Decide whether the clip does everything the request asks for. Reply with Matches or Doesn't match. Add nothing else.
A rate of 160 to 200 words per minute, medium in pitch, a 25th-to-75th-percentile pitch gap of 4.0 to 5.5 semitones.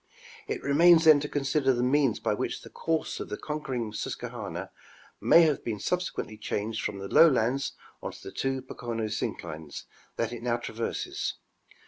Doesn't match